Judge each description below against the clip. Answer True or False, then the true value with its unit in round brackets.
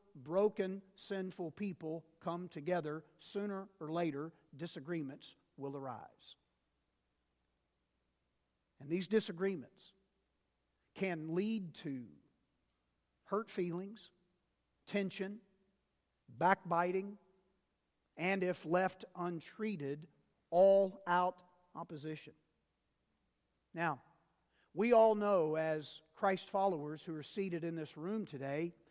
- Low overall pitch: False (170 Hz)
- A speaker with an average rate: False (85 wpm)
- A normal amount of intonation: True (4.7 semitones)